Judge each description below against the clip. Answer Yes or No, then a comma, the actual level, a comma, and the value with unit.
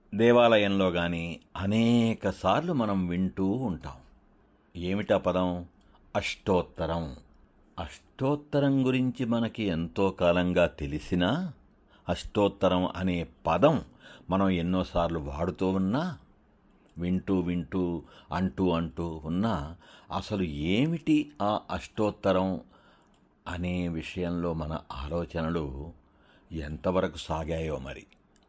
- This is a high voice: No, very low, 90 Hz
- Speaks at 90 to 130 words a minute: No, average, 80 wpm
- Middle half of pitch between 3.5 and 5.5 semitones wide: No, average, 2.8 semitones